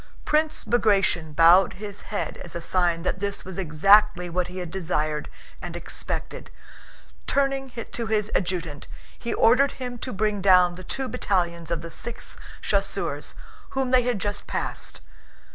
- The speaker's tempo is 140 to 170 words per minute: Yes, average, 155 wpm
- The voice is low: No, high, 195 Hz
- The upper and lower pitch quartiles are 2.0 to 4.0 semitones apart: No, average, 5.1 semitones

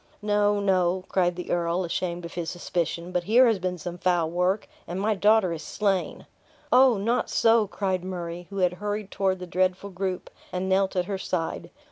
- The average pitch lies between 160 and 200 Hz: Yes, medium, 185 Hz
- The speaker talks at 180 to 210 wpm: Yes, average, 190 wpm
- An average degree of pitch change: No, narrow, 2.3 semitones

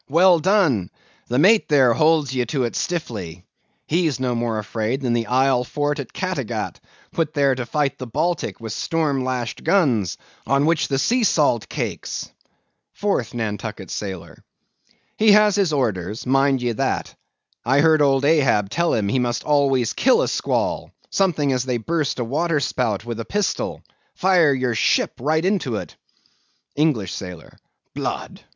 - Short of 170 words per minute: Yes, average, 160 wpm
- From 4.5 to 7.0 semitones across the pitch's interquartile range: Yes, average, 5.1 semitones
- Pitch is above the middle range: No, low, 135 Hz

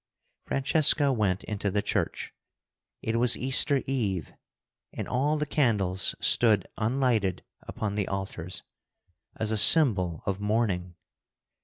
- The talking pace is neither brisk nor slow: No, slow, 120 wpm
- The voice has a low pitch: Yes, low, 110 Hz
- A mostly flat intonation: No, average, 5.1 semitones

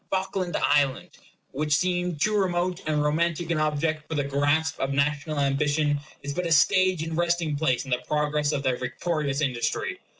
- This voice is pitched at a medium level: Yes, medium, 150 Hz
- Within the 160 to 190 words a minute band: Yes, average, 175 wpm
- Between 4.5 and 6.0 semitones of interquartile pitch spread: No, average, 3.2 semitones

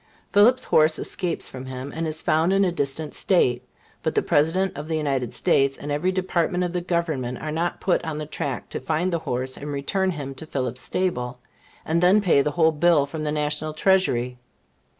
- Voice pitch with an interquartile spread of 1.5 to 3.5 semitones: No, average, 4.3 semitones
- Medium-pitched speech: Yes, medium, 155 Hz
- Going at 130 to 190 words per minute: No, average, 200 wpm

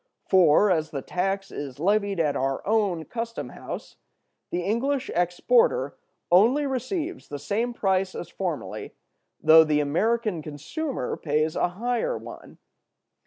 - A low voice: No, high, 190 Hz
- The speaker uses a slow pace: Yes, slow, 130 wpm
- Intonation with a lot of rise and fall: Yes, wide, 6.9 semitones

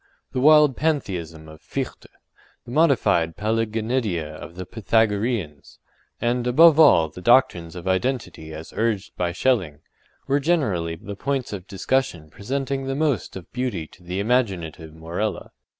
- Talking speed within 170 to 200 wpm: No, average, 140 wpm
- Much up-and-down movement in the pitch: Yes, wide, 7.3 semitones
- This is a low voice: Yes, low, 105 Hz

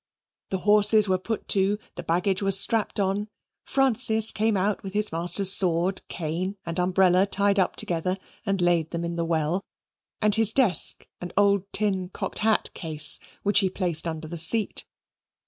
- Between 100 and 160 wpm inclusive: No, average, 170 wpm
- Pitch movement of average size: Yes, average, 3.0 semitones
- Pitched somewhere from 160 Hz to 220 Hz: Yes, high, 190 Hz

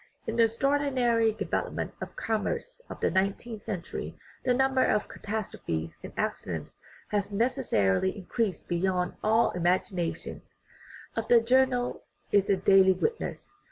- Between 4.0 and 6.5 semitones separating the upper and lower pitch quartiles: Yes, average, 4.5 semitones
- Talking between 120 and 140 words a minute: Yes, slow, 135 wpm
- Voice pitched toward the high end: Yes, high, 215 Hz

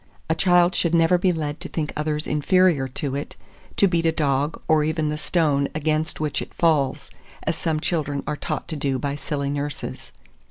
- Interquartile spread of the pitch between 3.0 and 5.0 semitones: No, narrow, 2.4 semitones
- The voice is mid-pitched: Yes, medium, 155 Hz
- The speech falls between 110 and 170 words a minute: No, average, 195 wpm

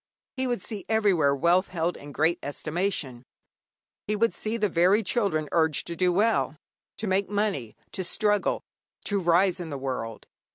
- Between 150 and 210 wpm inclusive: Yes, average, 165 wpm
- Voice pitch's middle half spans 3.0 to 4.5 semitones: No, average, 4.9 semitones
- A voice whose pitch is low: No, medium, 180 Hz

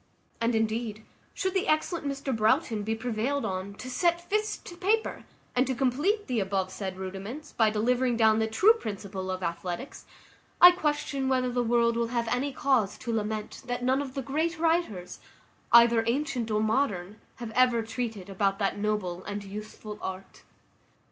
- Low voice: No, high, 235 Hz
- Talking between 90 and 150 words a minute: No, average, 170 wpm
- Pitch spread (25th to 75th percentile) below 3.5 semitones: No, average, 4.6 semitones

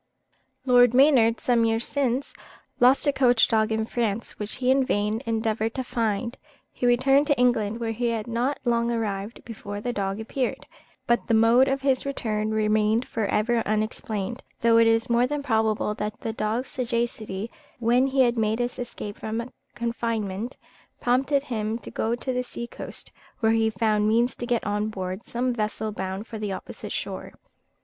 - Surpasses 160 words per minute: Yes, average, 180 wpm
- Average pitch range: No, narrow, 2.2 semitones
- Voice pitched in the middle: No, high, 230 Hz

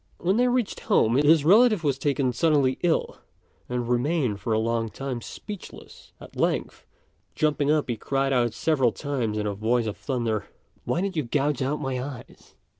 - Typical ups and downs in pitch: Yes, average, 4.4 semitones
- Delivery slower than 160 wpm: No, average, 180 wpm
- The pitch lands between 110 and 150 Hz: Yes, low, 135 Hz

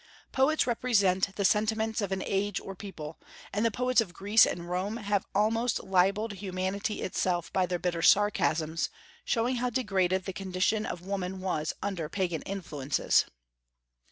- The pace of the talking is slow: No, average, 155 wpm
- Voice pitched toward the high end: Yes, high, 195 Hz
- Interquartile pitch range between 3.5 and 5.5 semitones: No, average, 3.0 semitones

